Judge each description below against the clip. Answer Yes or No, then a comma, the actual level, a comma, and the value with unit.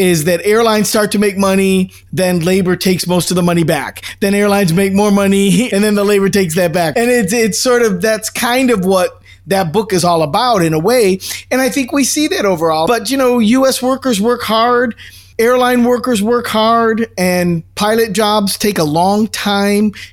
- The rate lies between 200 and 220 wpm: Yes, fast, 205 wpm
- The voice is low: No, high, 205 Hz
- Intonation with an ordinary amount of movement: Yes, average, 4.0 semitones